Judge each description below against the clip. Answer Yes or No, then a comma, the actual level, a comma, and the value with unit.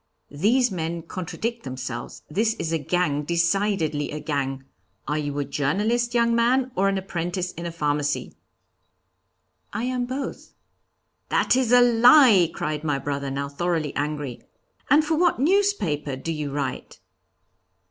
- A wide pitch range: Yes, wide, 8.1 semitones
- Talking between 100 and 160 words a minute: Yes, average, 145 wpm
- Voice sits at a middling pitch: Yes, medium, 170 Hz